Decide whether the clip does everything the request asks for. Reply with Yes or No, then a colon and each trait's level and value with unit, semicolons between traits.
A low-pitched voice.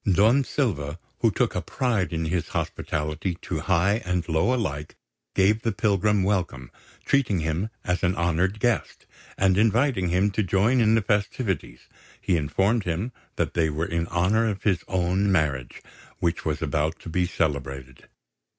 Yes: very low, 90 Hz